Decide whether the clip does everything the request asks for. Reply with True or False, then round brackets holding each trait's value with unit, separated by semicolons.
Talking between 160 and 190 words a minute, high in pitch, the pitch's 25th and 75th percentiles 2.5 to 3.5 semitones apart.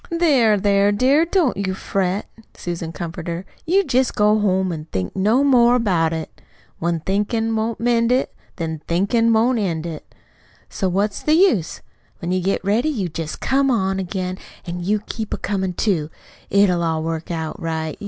False (175 wpm; 195 Hz; 5.2 semitones)